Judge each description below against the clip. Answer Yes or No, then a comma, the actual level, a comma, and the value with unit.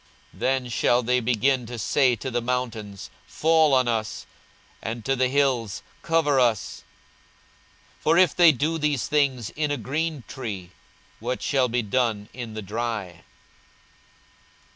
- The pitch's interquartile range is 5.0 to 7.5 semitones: No, average, 3.8 semitones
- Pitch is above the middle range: No, low, 125 Hz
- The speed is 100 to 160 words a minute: Yes, average, 150 wpm